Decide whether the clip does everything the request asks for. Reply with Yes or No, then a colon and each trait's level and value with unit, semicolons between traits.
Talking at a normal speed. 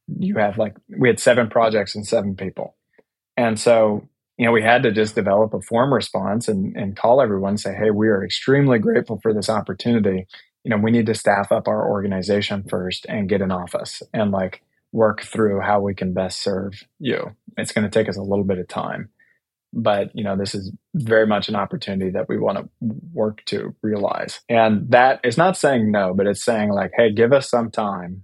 No: fast, 215 wpm